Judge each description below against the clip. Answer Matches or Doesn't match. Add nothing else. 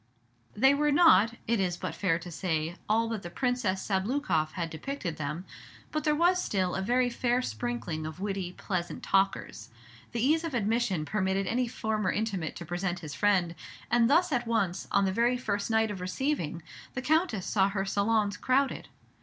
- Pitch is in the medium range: Doesn't match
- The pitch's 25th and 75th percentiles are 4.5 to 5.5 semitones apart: Matches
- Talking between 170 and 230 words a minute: Matches